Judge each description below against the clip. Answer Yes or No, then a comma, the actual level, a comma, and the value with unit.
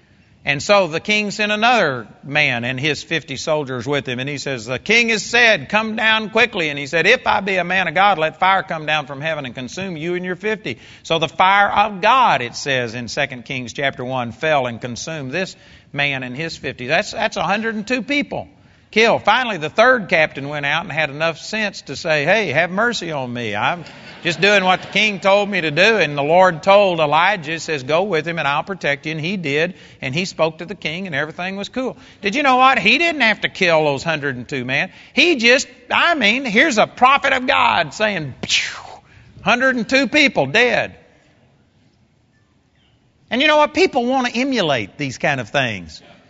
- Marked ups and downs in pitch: Yes, wide, 6.8 semitones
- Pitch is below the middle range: No, medium, 175 Hz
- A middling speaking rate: No, fast, 210 wpm